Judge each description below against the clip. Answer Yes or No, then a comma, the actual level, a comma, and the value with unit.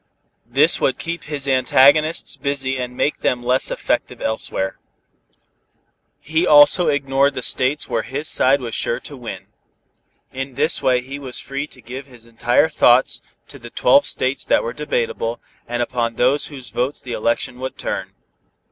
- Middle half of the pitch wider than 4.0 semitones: No, average, 2.7 semitones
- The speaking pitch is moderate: No, low, 130 Hz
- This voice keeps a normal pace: Yes, average, 160 wpm